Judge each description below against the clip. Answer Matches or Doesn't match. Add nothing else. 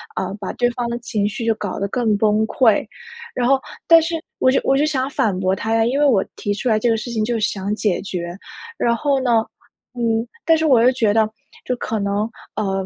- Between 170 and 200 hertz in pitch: Doesn't match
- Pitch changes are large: Doesn't match